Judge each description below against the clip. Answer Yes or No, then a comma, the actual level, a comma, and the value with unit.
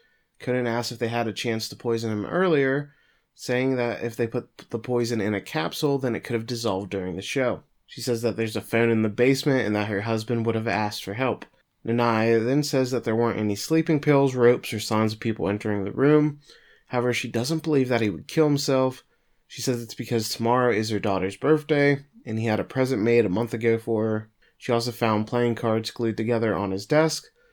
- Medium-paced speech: No, fast, 225 wpm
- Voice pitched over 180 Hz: No, low, 120 Hz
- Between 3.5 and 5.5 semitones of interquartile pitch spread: No, average, 2.9 semitones